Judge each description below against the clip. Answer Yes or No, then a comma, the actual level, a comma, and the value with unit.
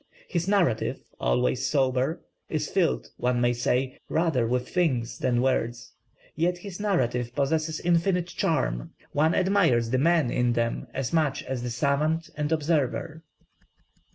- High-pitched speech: No, medium, 140 Hz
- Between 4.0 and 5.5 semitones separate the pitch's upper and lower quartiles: Yes, average, 5.2 semitones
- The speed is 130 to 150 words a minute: Yes, average, 140 wpm